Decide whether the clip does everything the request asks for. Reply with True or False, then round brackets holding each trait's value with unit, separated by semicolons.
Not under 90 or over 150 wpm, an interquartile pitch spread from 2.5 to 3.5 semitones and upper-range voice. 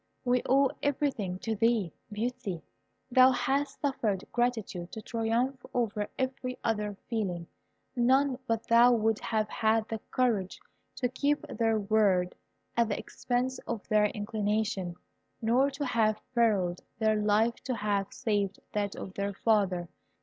True (140 wpm; 3.2 semitones; 225 Hz)